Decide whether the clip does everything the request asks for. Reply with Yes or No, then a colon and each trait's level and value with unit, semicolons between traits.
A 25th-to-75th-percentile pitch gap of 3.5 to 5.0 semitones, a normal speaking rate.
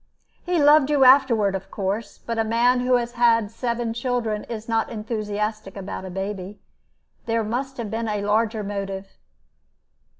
No: average, 2.7 semitones; average, 160 wpm